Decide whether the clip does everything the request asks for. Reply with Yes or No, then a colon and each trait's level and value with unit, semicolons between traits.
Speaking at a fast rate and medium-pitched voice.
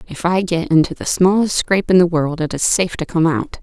Yes: fast, 265 wpm; medium, 175 Hz